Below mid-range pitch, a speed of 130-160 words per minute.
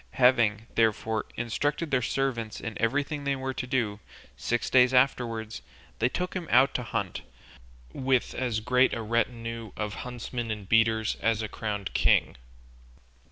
Yes: low, 115 Hz; average, 150 wpm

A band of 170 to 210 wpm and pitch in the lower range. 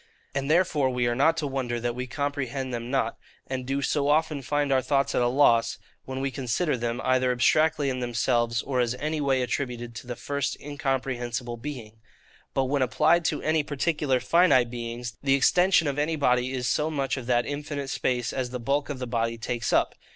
Yes: fast, 205 wpm; low, 130 Hz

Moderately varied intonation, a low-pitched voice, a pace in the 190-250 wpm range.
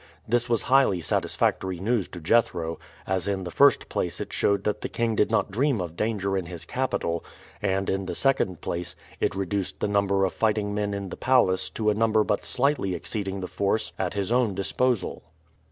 Yes: average, 3.1 semitones; low, 100 Hz; average, 200 wpm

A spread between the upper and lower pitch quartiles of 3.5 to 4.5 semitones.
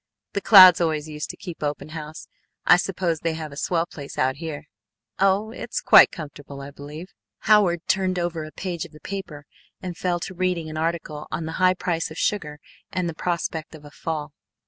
No: average, 3.1 semitones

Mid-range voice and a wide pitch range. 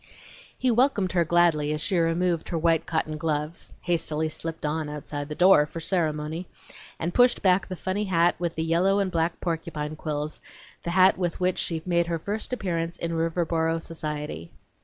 No: medium, 165 Hz; narrow, 2.5 semitones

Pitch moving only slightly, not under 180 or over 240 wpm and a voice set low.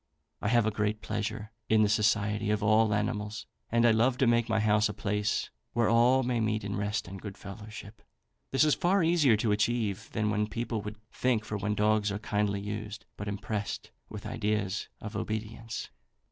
Yes: narrow, 1.5 semitones; average, 190 wpm; low, 105 Hz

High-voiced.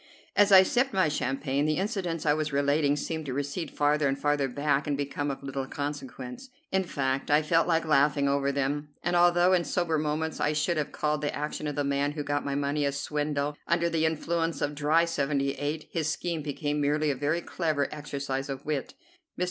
No: medium, 150 Hz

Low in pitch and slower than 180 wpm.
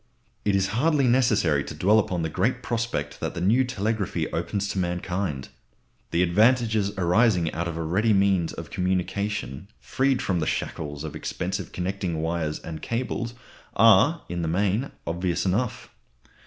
Yes: very low, 95 Hz; average, 155 wpm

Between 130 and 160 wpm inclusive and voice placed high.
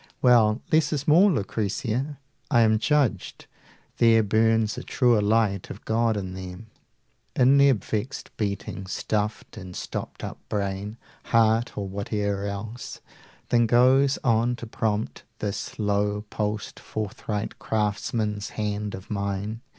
No: slow, 135 wpm; low, 110 Hz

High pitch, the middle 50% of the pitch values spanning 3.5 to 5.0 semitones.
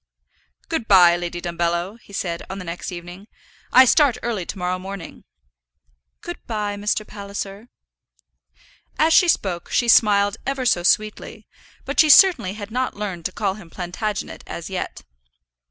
Yes: high, 200 Hz; average, 4.1 semitones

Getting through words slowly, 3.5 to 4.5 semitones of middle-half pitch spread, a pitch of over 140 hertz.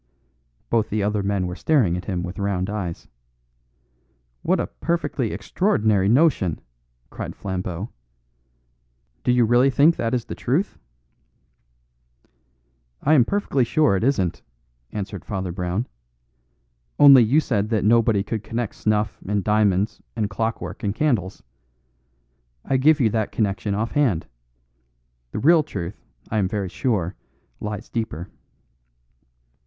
No: slow, 130 wpm; average, 4.2 semitones; low, 105 Hz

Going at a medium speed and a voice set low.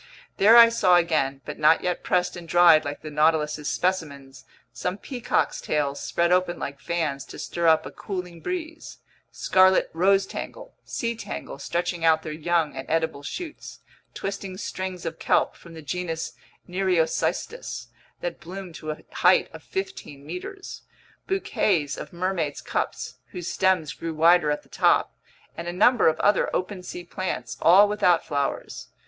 No: average, 155 wpm; medium, 175 Hz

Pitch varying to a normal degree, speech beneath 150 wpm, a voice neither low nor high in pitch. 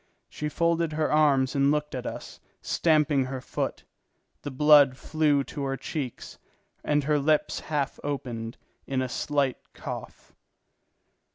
No: narrow, 2.1 semitones; average, 140 wpm; medium, 145 Hz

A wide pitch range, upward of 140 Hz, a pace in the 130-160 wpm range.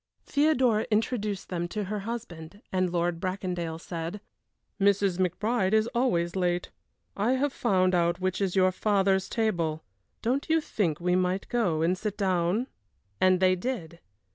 No: average, 3.6 semitones; high, 190 Hz; average, 150 wpm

